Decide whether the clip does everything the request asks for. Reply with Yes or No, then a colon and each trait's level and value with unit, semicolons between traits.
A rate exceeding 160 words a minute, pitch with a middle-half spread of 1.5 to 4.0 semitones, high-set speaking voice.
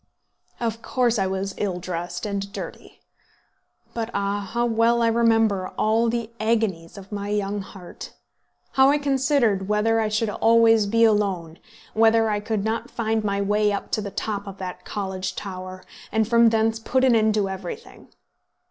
Yes: average, 170 wpm; narrow, 2.5 semitones; high, 215 Hz